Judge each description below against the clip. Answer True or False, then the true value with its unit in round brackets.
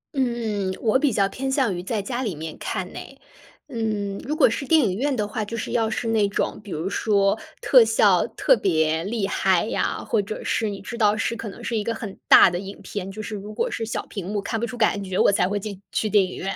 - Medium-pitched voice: False (210 Hz)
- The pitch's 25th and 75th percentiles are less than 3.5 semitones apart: True (2.8 semitones)